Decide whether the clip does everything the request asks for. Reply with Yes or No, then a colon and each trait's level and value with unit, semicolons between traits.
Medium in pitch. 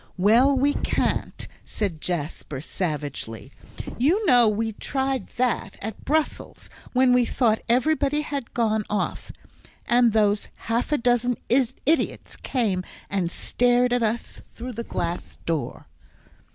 No: high, 235 Hz